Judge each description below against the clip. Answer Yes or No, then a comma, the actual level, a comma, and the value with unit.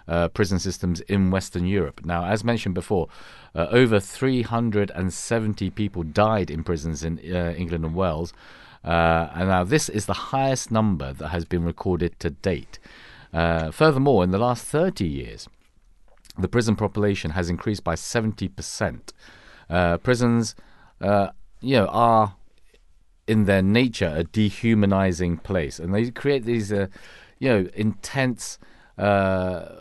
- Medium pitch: No, very low, 95 Hz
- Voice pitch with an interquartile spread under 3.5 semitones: No, average, 4.1 semitones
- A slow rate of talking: No, average, 145 wpm